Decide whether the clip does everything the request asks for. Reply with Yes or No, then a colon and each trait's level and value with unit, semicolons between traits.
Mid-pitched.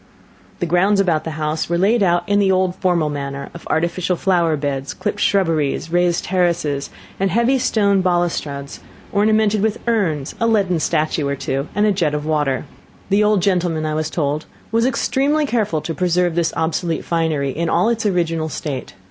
Yes: medium, 175 Hz